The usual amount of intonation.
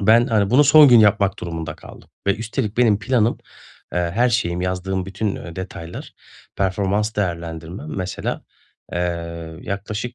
Yes: average, 3.9 semitones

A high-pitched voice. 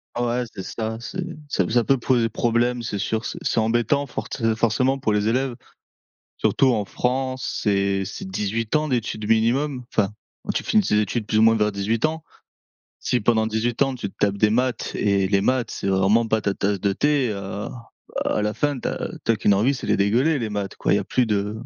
No: low, 115 Hz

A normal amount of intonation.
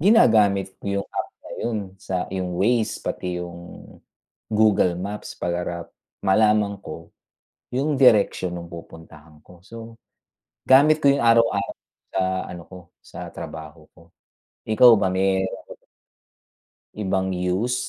Yes: average, 4.1 semitones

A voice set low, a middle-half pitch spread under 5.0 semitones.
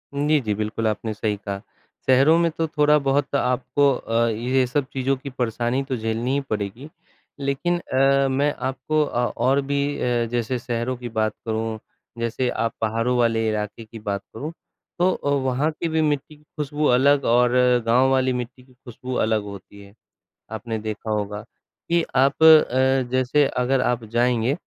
Yes: low, 125 Hz; average, 3.5 semitones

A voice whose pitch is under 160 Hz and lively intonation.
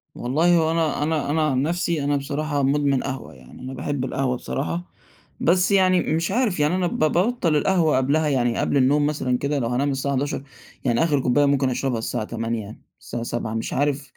No: medium, 140 Hz; average, 3.6 semitones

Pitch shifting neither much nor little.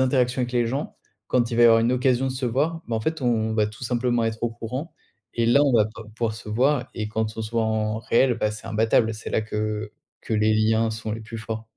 No: narrow, 2.1 semitones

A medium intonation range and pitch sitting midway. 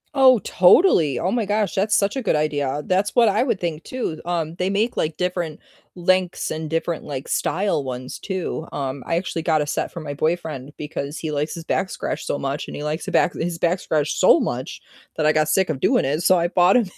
Yes: average, 3.7 semitones; medium, 165 Hz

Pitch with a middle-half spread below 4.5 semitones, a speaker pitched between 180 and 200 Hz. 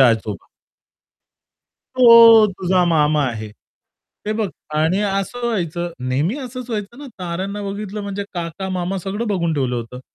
No: average, 4.9 semitones; high, 190 Hz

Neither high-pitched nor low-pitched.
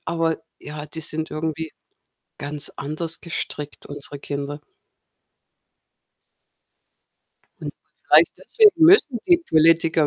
Yes: medium, 160 Hz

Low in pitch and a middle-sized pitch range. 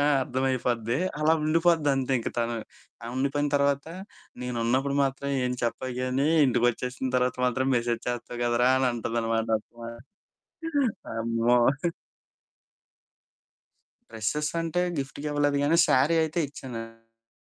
Yes: low, 130 Hz; average, 3.2 semitones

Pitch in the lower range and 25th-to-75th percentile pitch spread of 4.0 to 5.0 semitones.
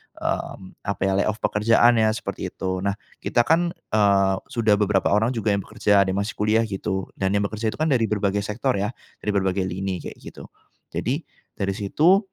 No: low, 105 Hz; narrow, 2.5 semitones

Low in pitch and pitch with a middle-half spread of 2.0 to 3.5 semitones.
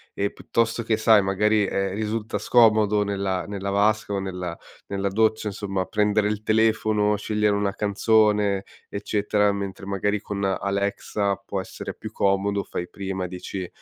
No: low, 100 Hz; narrow, 1.4 semitones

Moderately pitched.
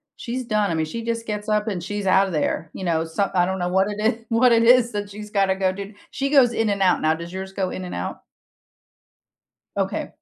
No: high, 200 Hz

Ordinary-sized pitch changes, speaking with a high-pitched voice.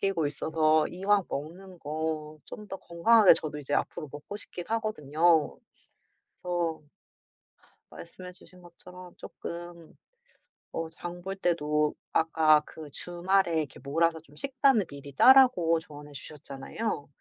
No: average, 3.2 semitones; medium, 165 Hz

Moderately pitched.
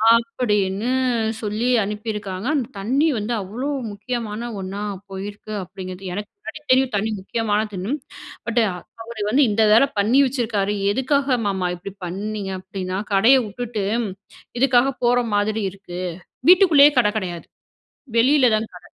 No: high, 215 Hz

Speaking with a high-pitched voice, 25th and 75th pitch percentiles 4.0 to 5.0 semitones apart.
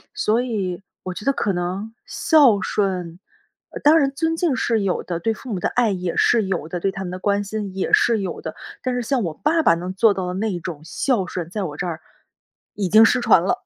Yes: high, 200 Hz; average, 4.7 semitones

